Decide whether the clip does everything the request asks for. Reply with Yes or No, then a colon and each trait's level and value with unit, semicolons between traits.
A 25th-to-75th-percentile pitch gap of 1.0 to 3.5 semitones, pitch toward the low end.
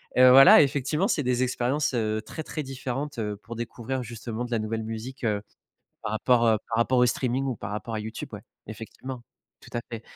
Yes: average, 2.9 semitones; low, 120 Hz